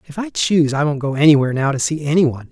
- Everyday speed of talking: No, fast, 285 wpm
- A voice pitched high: No, medium, 150 Hz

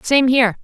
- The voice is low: No, very high, 250 Hz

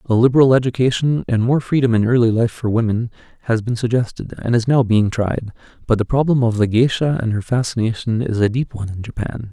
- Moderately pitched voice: No, low, 120 Hz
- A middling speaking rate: No, fast, 215 wpm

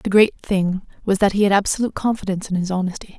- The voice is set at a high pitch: Yes, high, 195 Hz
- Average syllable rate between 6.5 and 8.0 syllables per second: Yes, 6.7 syllables/s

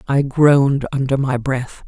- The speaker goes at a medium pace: Yes, average, 160 wpm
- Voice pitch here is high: No, low, 135 Hz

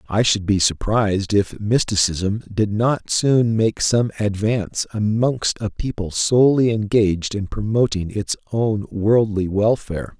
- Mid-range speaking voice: No, low, 105 Hz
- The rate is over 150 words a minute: No, slow, 135 wpm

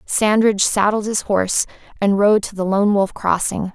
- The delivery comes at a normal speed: Yes, average, 175 wpm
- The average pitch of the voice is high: Yes, high, 200 Hz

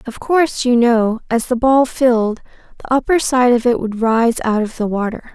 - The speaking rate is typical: No, fast, 215 wpm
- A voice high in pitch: Yes, high, 240 Hz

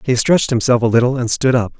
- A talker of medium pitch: No, low, 125 Hz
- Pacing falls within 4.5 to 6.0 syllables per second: No, 6.6 syllables/s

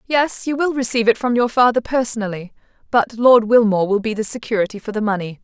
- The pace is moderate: No, fast, 210 wpm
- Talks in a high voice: Yes, high, 230 Hz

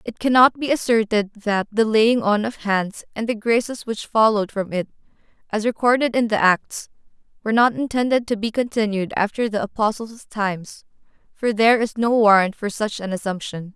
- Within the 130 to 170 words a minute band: No, average, 180 wpm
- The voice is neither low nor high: No, high, 220 Hz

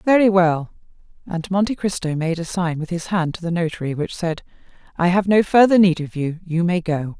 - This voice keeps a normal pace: No, fast, 215 wpm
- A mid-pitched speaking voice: Yes, medium, 175 Hz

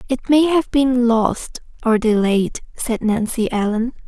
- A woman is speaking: Yes, female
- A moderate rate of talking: Yes, average, 145 wpm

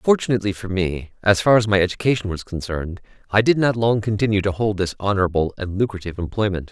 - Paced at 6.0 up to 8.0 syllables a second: Yes, 6.6 syllables/s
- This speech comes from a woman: No, male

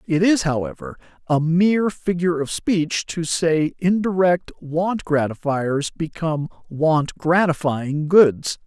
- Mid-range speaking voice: Yes, medium, 165 Hz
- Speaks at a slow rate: Yes, slow, 120 wpm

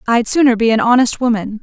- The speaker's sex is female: Yes, female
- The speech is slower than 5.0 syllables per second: No, 6.1 syllables/s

